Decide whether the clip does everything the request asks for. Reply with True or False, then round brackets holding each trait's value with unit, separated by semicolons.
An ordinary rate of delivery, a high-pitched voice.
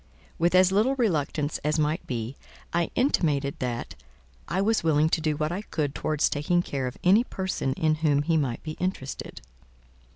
False (175 wpm; 155 Hz)